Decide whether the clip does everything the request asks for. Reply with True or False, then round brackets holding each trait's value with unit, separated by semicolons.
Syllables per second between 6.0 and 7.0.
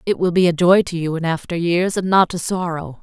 False (5.5 syllables/s)